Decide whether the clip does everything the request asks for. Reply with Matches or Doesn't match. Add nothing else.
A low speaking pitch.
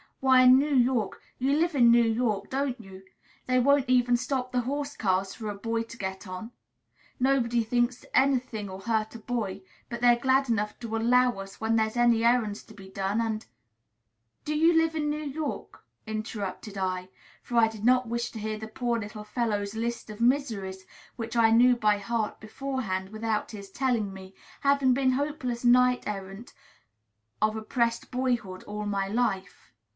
Doesn't match